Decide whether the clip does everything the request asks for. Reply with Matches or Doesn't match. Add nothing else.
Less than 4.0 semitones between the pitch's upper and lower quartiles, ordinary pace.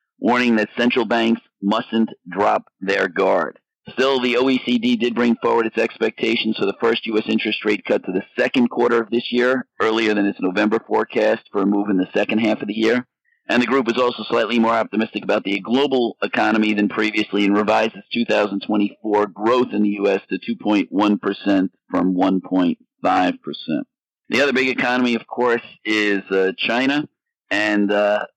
Matches